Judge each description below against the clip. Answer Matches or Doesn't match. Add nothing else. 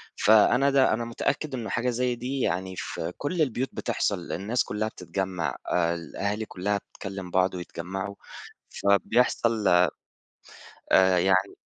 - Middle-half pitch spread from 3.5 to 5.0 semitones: Matches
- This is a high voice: Doesn't match